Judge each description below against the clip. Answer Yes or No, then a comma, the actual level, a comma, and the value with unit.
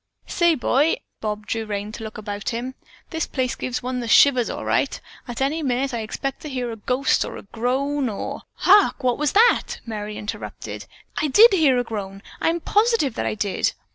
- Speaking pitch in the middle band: No, very high, 250 Hz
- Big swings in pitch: No, average, 4.8 semitones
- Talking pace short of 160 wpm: No, average, 200 wpm